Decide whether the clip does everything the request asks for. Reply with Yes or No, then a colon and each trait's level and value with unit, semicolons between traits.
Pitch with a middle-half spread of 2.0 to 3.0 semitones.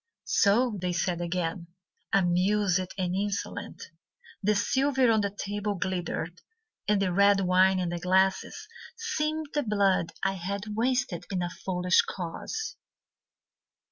Yes: narrow, 2.6 semitones